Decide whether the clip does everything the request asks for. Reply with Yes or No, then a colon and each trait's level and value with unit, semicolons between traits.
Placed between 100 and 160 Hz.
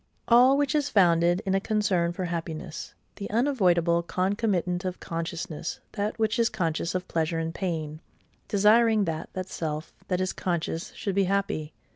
No: medium, 185 Hz